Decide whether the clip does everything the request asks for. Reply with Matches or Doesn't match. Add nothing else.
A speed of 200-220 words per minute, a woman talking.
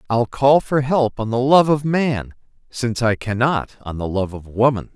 Doesn't match